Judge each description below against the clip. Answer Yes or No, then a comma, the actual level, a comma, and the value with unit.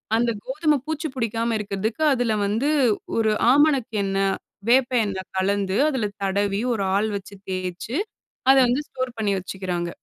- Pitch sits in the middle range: No, high, 220 Hz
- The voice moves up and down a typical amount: Yes, average, 4.6 semitones